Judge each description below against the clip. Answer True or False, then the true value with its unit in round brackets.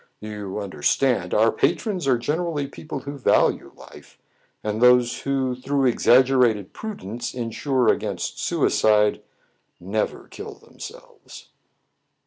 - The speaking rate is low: True (120 wpm)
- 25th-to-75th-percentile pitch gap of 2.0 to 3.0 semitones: False (4.2 semitones)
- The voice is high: False (125 Hz)